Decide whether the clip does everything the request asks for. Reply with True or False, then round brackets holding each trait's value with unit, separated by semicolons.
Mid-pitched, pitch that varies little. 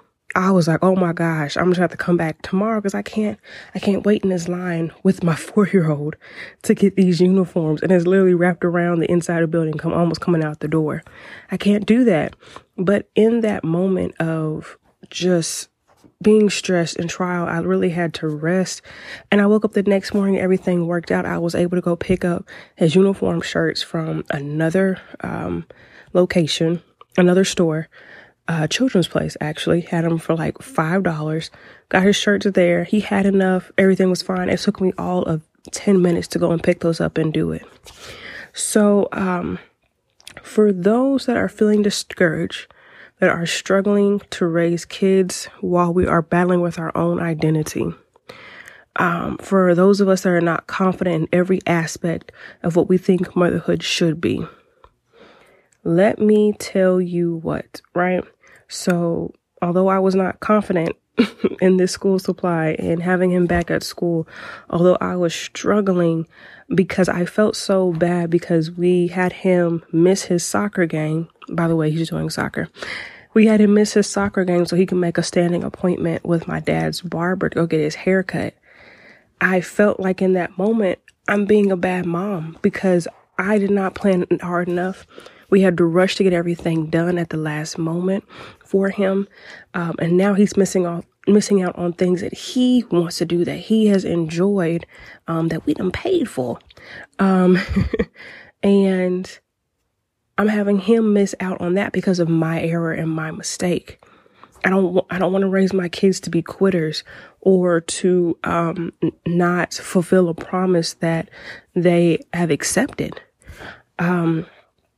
True (180 Hz; 2.3 semitones)